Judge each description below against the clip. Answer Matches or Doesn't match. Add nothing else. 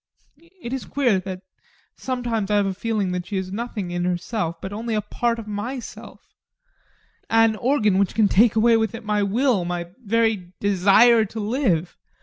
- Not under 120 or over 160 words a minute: Doesn't match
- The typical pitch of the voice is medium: Doesn't match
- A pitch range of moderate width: Matches